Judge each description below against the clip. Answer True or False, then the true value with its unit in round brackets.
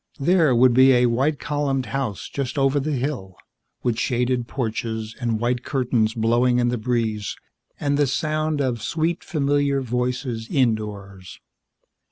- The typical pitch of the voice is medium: False (125 Hz)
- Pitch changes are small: False (3.2 semitones)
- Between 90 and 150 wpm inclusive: True (145 wpm)